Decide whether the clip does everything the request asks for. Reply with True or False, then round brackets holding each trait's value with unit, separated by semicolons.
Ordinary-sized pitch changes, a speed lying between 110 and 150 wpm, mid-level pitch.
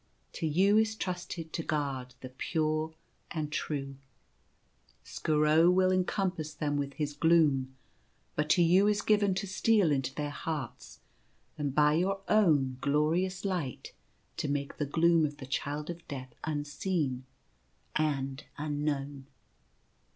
True (3.7 semitones; 140 wpm; 155 Hz)